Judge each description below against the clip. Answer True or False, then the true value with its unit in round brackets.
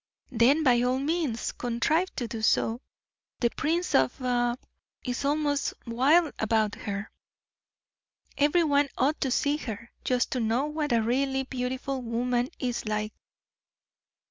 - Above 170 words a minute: False (140 wpm)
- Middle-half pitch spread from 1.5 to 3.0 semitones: False (3.6 semitones)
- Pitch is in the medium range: False (255 Hz)